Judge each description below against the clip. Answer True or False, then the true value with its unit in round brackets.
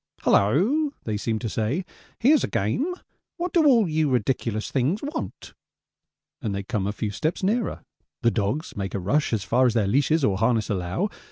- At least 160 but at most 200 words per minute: True (185 wpm)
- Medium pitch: False (125 Hz)